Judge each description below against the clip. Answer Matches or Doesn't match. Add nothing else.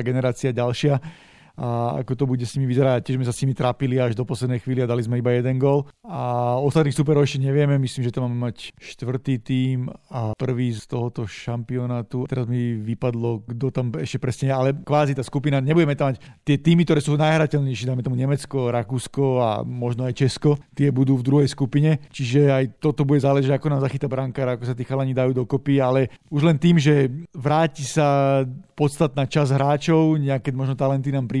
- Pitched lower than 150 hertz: Matches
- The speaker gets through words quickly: Matches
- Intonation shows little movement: Matches